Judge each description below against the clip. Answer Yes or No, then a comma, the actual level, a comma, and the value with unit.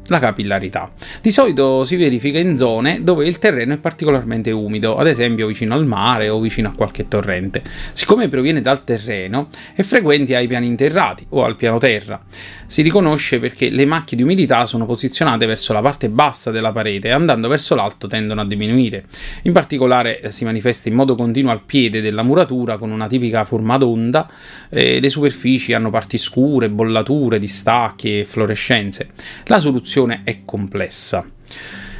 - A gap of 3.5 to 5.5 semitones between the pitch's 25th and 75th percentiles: Yes, average, 4.2 semitones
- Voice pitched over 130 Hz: No, low, 120 Hz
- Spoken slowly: No, average, 165 wpm